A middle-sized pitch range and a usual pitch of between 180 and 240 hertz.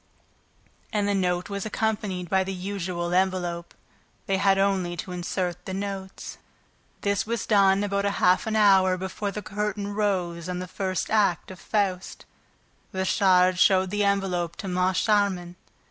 No: narrow, 1.9 semitones; high, 190 Hz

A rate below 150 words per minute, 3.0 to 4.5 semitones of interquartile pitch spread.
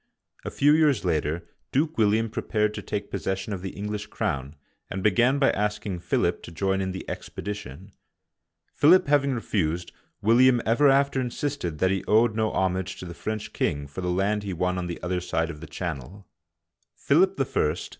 No: average, 185 wpm; average, 4.2 semitones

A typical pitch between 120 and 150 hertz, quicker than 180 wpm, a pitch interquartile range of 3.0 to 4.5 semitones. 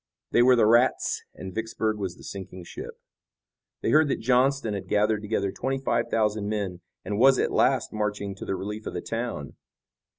No: low, 110 Hz; average, 190 wpm; average, 3.3 semitones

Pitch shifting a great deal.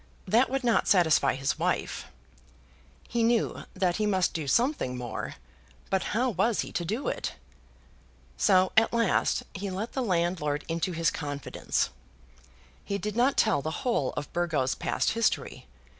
Yes: wide, 6.2 semitones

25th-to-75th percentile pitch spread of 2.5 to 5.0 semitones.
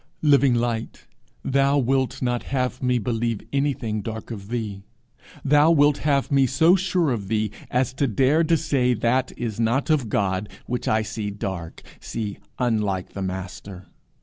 Yes: average, 4.4 semitones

